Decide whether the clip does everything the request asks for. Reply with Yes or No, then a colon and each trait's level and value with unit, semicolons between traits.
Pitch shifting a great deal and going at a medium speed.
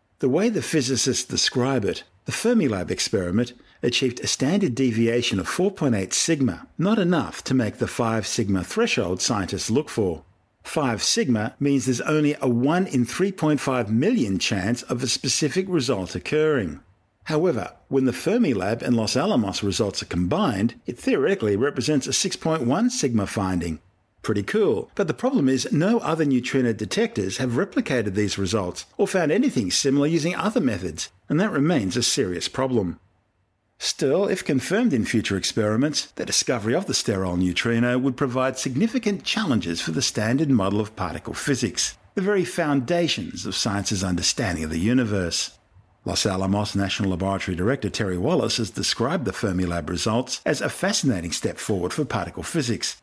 Yes: wide, 6.9 semitones; average, 155 wpm